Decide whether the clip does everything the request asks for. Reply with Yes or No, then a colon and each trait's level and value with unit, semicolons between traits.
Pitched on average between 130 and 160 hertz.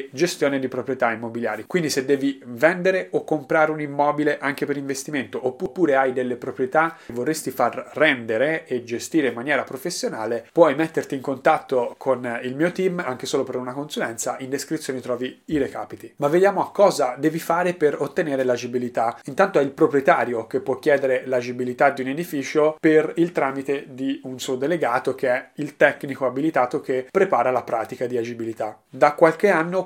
Yes: medium, 140 Hz